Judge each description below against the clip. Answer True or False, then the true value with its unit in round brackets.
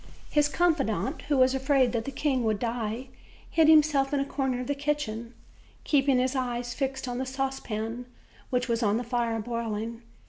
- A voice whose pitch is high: True (255 Hz)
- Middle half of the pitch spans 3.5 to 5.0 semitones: False (3.0 semitones)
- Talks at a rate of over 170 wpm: True (180 wpm)